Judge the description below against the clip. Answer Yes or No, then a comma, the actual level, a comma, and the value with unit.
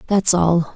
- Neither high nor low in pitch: Yes, medium, 175 Hz